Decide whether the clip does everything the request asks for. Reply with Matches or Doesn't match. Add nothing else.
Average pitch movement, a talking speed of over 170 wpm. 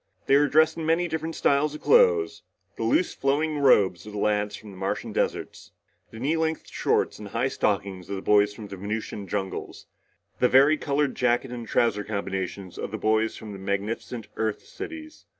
Doesn't match